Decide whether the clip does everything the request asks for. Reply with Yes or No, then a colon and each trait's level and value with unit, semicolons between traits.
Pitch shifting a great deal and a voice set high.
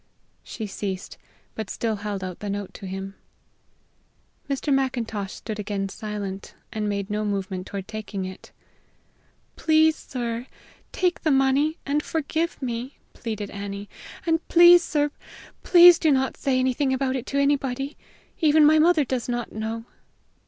Yes: wide, 6.0 semitones; high, 240 Hz